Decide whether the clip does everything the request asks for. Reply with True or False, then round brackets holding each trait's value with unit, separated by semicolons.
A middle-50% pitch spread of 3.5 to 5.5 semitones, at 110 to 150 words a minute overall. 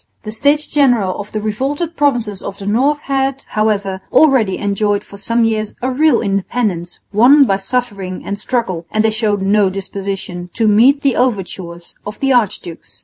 False (4.6 semitones; 170 wpm)